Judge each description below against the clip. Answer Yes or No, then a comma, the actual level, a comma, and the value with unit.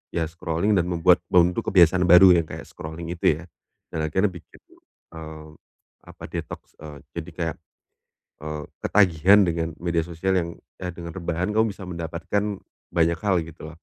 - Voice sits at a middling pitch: No, very low, 85 Hz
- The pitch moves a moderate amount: No, narrow, 2.2 semitones